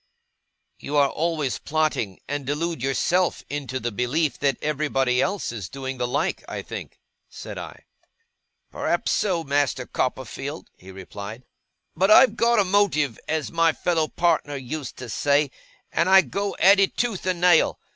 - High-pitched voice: No, medium, 145 Hz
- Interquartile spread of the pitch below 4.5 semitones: No, average, 4.8 semitones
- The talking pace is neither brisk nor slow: Yes, average, 155 wpm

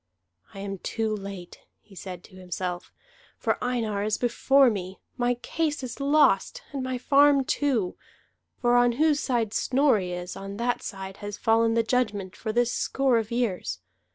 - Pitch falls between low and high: No, high, 225 Hz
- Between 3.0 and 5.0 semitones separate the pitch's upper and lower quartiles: Yes, average, 4.4 semitones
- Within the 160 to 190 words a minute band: Yes, average, 165 wpm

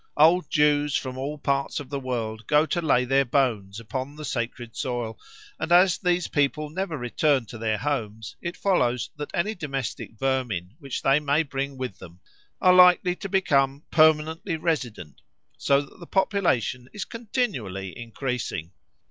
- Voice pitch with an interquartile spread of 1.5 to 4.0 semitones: No, average, 4.9 semitones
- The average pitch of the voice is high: No, medium, 140 Hz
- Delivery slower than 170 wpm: Yes, average, 160 wpm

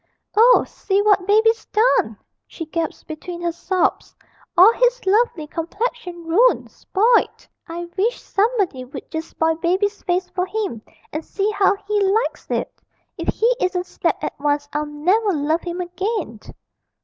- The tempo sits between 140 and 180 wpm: Yes, average, 150 wpm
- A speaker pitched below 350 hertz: No, very high, 370 Hz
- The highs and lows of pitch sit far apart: No, average, 4.5 semitones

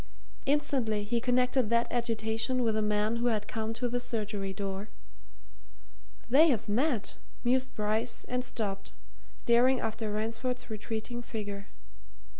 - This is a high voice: Yes, high, 225 Hz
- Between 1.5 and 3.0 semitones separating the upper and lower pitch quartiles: Yes, narrow, 2.6 semitones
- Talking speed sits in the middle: No, slow, 125 wpm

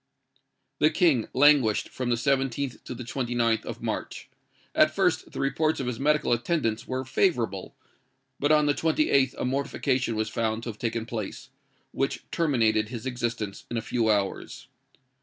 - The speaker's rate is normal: Yes, average, 160 wpm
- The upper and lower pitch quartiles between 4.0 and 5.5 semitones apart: No, average, 3.6 semitones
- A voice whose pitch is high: No, low, 125 Hz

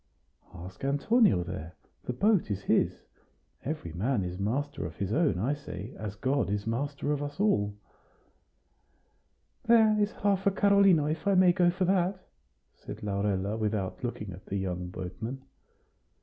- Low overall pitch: Yes, low, 125 Hz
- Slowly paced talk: No, average, 155 wpm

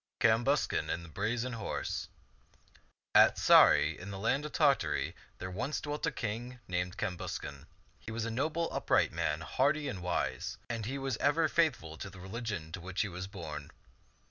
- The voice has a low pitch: Yes, low, 110 Hz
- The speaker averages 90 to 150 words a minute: No, average, 170 wpm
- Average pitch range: No, wide, 6.9 semitones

